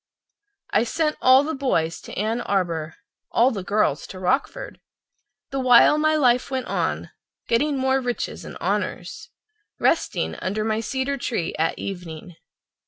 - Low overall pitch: No, high, 235 Hz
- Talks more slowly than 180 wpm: Yes, average, 150 wpm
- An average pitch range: No, wide, 6.3 semitones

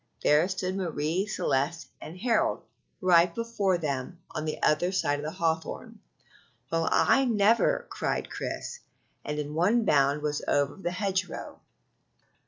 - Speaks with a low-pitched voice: No, medium, 170 Hz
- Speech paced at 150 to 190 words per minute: No, average, 140 wpm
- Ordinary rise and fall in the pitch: Yes, average, 4.6 semitones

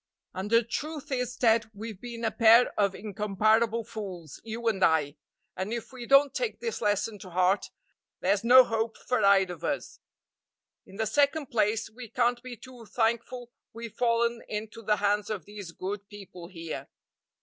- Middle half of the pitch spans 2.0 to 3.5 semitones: Yes, average, 2.9 semitones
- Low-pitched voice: No, high, 220 Hz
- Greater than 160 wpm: Yes, average, 170 wpm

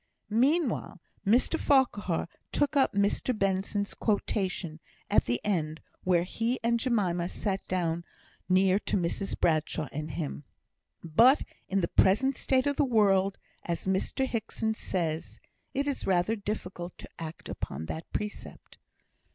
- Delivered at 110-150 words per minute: Yes, slow, 135 wpm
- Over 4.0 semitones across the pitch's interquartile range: Yes, average, 5.1 semitones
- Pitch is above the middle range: Yes, high, 195 Hz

